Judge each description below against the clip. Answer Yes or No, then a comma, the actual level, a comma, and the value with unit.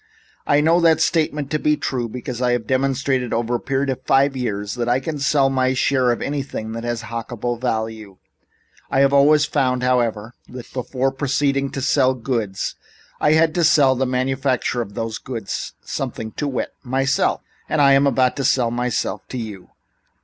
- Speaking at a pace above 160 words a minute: Yes, average, 185 wpm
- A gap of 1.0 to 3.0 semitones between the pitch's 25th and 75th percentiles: Yes, narrow, 2.5 semitones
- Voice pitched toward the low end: Yes, low, 130 Hz